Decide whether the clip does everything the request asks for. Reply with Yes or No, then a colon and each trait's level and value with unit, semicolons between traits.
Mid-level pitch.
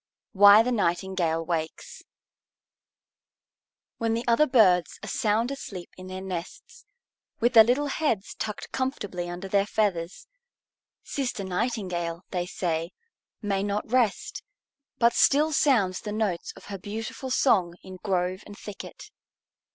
No: high, 200 Hz